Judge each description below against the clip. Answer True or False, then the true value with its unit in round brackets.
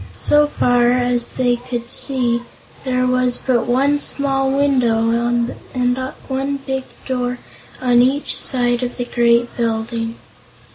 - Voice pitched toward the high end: True (245 Hz)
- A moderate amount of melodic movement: False (1.8 semitones)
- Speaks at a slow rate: True (130 wpm)